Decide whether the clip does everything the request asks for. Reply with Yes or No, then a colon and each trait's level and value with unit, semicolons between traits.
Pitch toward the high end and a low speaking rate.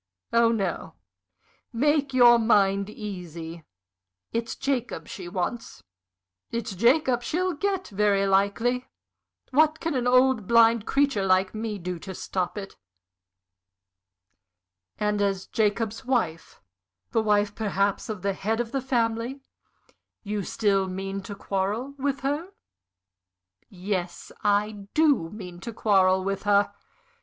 Yes: high, 210 Hz; slow, 125 wpm